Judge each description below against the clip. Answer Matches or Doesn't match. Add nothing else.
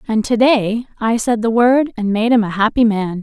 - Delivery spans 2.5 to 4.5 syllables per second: Doesn't match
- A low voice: Doesn't match